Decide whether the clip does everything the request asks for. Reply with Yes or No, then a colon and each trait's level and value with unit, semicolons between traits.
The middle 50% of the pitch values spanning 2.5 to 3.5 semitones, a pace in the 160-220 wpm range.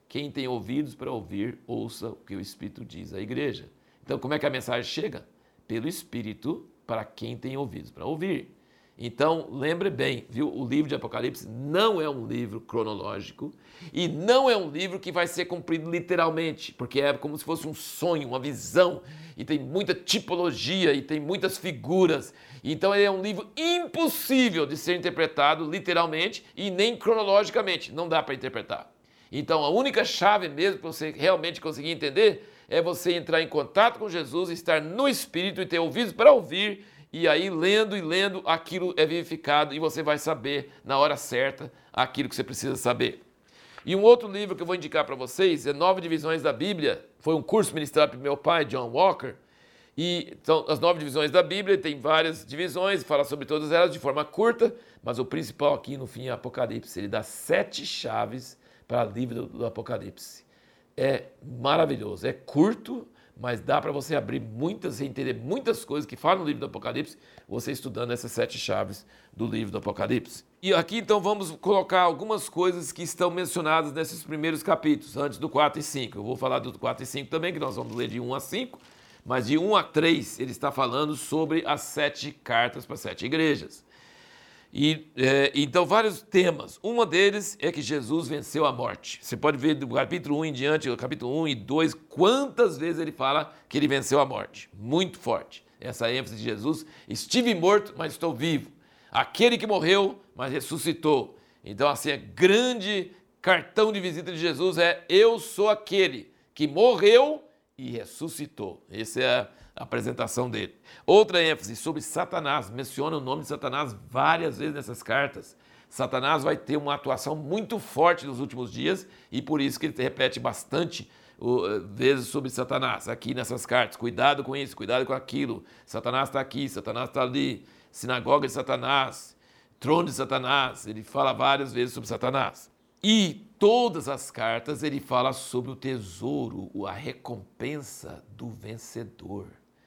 No: average, 4.9 semitones; average, 180 wpm